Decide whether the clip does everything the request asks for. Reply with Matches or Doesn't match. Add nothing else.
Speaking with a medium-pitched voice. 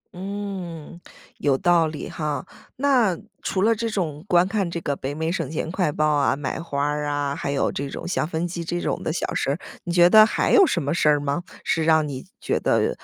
Matches